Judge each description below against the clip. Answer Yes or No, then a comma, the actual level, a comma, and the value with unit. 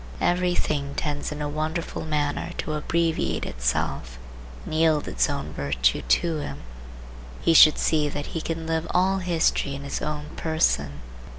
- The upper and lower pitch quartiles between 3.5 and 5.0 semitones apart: No, narrow, 2.5 semitones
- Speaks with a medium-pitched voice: Yes, medium, 150 Hz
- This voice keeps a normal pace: Yes, average, 160 wpm